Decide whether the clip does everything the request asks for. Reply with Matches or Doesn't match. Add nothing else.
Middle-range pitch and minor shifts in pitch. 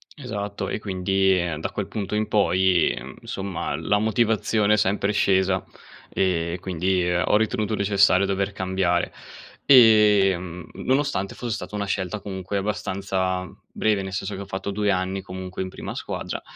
Doesn't match